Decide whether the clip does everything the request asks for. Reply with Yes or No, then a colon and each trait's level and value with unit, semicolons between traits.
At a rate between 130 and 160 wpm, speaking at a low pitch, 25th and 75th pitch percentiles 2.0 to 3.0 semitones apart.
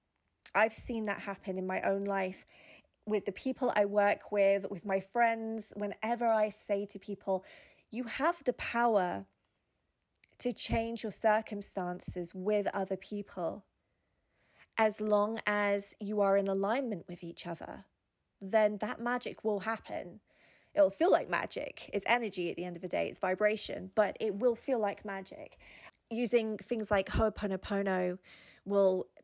No: average, 150 wpm; high, 205 Hz; narrow, 2.6 semitones